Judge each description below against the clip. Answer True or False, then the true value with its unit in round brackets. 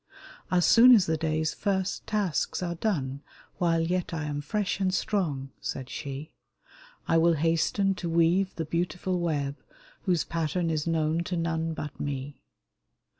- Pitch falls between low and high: True (165 Hz)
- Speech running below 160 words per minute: False (165 wpm)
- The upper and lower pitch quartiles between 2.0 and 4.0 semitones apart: True (3.0 semitones)